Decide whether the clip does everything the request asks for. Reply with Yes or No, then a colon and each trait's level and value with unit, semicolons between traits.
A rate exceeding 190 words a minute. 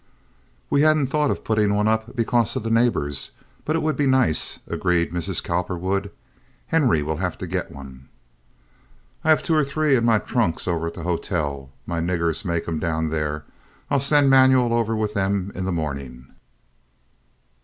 No: average, 175 wpm